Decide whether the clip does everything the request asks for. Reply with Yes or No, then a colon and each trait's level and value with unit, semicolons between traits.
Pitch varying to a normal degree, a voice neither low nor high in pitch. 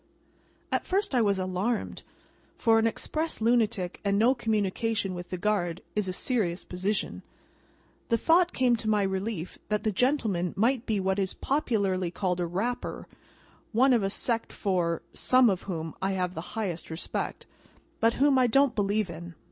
No: average, 4.3 semitones; high, 210 Hz